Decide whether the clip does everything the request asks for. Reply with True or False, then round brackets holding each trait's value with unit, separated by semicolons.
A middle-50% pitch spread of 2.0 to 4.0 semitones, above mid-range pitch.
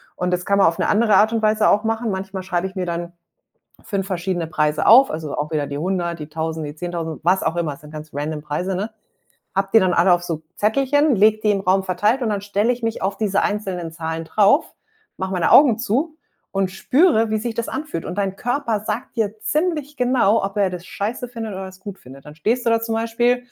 False (4.6 semitones; 195 Hz)